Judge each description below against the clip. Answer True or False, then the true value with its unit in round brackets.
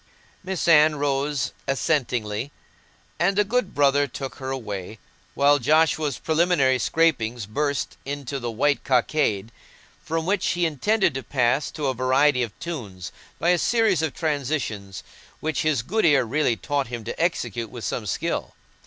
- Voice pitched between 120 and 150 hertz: True (140 Hz)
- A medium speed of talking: True (155 wpm)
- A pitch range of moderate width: True (4.6 semitones)